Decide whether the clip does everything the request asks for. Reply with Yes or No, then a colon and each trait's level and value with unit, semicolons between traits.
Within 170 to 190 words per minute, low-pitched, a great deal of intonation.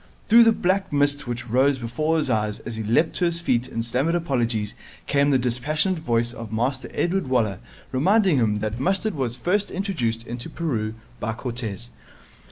Yes: average, 175 wpm; low, 130 Hz; wide, 6.2 semitones